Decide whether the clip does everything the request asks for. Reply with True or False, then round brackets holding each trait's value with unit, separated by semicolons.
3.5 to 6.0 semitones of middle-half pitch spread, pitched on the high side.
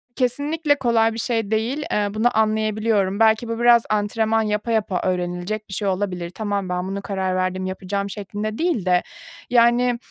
False (3.1 semitones; 215 Hz)